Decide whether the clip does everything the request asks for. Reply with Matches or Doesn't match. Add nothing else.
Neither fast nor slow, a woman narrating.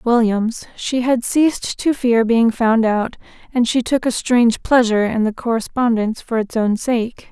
Matches